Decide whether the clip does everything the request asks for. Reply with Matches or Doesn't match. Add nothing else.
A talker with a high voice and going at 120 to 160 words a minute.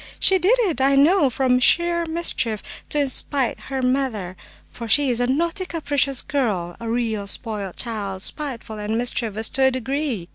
Doesn't match